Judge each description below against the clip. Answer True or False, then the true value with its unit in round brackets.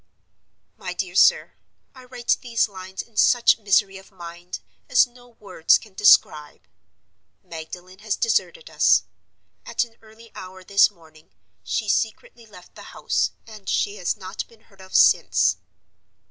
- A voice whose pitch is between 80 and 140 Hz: False (205 Hz)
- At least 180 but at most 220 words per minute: False (145 wpm)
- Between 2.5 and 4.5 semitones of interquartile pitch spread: True (3.6 semitones)